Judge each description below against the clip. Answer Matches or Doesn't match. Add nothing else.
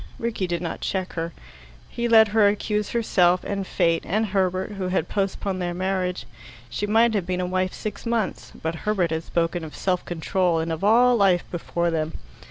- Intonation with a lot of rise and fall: Doesn't match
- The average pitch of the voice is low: Doesn't match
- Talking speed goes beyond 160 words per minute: Matches